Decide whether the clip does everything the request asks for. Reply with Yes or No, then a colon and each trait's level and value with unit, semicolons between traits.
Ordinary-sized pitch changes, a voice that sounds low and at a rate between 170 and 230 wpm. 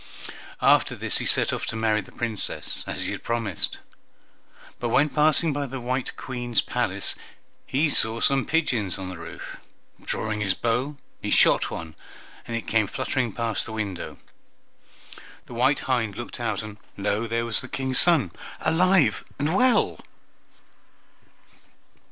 No: average, 3.9 semitones; low, 120 Hz; average, 150 wpm